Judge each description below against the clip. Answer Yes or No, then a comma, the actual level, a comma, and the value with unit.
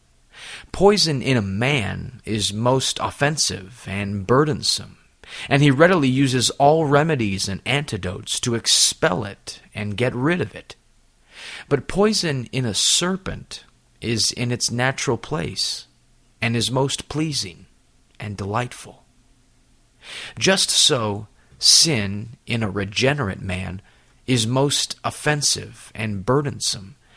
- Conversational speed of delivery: No, slow, 115 wpm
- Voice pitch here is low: Yes, low, 120 Hz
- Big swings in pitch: Yes, wide, 5.8 semitones